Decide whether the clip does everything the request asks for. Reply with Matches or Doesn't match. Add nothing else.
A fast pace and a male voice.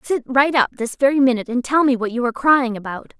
Doesn't match